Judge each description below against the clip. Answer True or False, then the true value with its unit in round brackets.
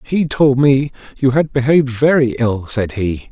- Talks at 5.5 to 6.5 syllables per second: False (4.4 syllables/s)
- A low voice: True (130 Hz)